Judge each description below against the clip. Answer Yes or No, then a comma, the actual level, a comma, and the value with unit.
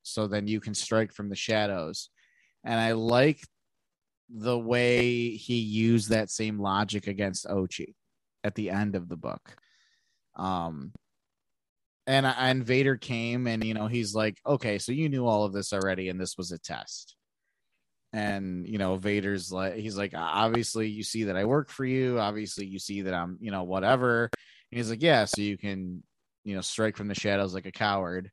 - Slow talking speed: No, average, 185 wpm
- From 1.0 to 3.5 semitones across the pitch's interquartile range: Yes, average, 3.1 semitones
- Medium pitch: No, low, 105 Hz